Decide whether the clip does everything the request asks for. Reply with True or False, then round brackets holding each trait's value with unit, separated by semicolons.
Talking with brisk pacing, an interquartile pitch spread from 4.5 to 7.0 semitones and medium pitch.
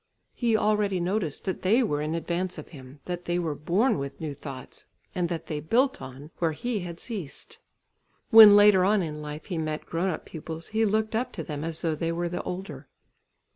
True (210 wpm; 5.0 semitones; 175 Hz)